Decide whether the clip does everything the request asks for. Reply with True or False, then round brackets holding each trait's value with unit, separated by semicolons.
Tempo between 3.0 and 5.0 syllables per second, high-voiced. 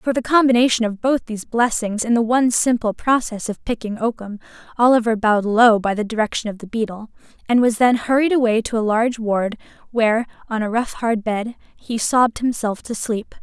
False (5.5 syllables/s; 230 Hz)